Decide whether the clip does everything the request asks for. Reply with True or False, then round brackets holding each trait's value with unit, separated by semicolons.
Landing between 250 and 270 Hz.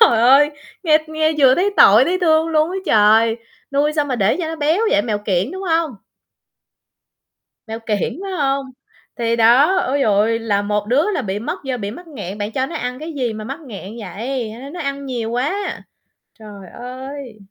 True (255 Hz)